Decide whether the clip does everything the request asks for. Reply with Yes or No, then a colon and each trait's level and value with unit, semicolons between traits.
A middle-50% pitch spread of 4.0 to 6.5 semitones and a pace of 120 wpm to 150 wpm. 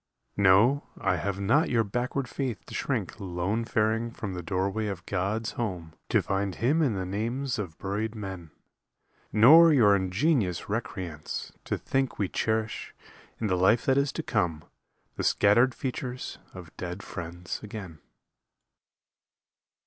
Yes: average, 4.5 semitones; average, 145 wpm